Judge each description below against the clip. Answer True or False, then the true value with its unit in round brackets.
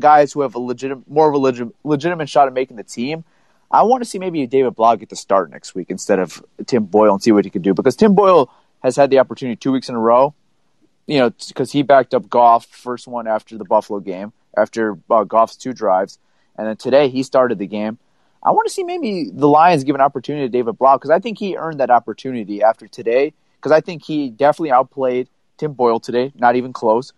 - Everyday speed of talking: False (240 wpm)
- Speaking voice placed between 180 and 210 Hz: False (130 Hz)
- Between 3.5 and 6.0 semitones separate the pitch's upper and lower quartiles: True (4.4 semitones)